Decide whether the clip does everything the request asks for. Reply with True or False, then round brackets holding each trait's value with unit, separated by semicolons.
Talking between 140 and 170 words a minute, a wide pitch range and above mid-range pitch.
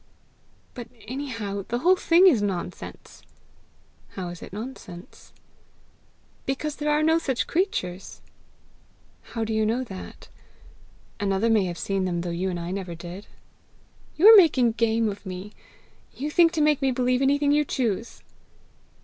True (150 wpm; 7.0 semitones; 230 Hz)